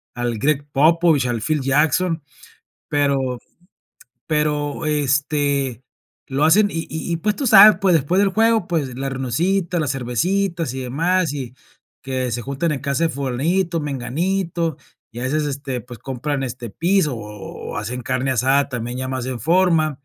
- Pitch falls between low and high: Yes, medium, 145 Hz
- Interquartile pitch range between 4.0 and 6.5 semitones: Yes, average, 4.5 semitones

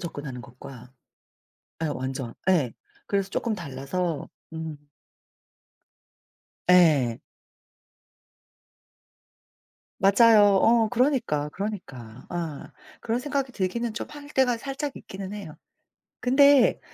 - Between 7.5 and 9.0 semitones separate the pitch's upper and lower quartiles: Yes, wide, 8.6 semitones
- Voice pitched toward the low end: No, high, 190 Hz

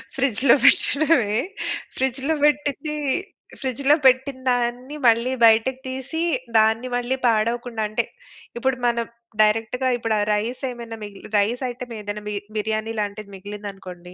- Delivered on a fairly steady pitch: No, average, 3.4 semitones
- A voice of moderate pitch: No, high, 235 Hz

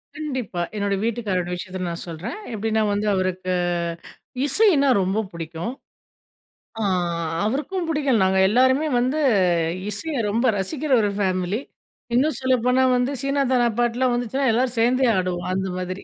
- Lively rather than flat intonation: Yes, wide, 5.8 semitones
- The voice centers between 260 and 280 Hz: No, high, 235 Hz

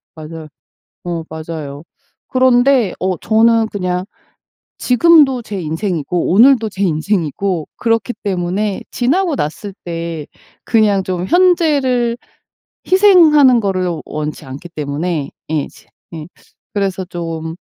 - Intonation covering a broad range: Yes, wide, 6.8 semitones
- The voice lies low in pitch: No, high, 190 Hz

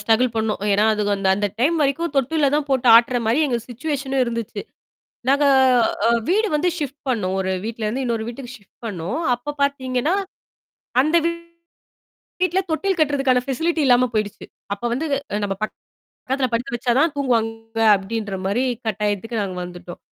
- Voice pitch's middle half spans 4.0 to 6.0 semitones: Yes, average, 4.3 semitones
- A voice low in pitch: No, high, 245 Hz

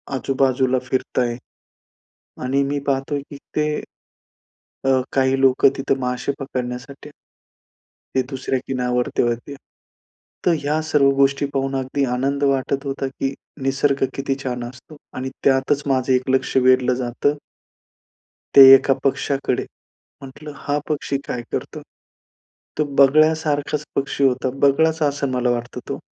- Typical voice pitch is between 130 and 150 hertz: Yes, low, 135 Hz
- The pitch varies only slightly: Yes, narrow, 1.6 semitones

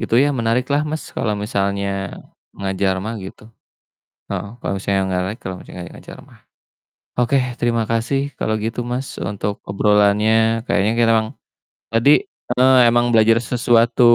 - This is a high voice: No, low, 115 Hz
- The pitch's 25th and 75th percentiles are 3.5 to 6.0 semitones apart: No, average, 2.9 semitones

